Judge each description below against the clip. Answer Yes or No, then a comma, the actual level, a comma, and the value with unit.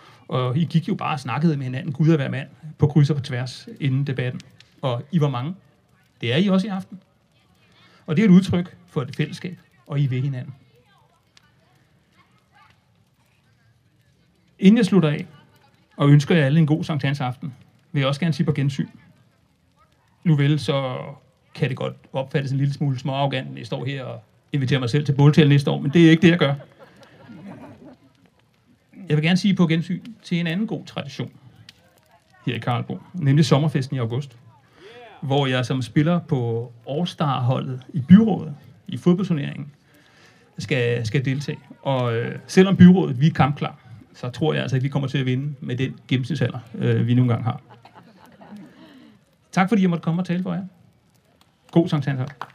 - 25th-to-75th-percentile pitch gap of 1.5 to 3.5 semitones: No, average, 4.0 semitones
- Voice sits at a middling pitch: Yes, medium, 145 Hz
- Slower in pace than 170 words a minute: No, average, 180 wpm